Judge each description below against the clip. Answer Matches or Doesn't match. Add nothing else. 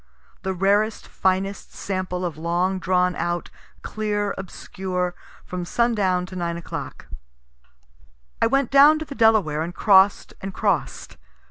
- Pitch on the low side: Doesn't match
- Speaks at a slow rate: Matches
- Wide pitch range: Doesn't match